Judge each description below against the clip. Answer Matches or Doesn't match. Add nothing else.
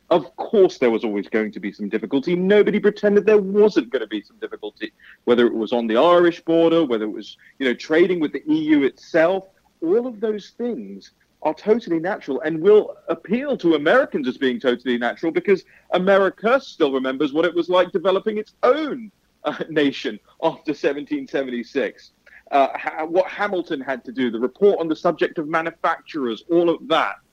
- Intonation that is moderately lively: Doesn't match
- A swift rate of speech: Doesn't match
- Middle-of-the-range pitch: Matches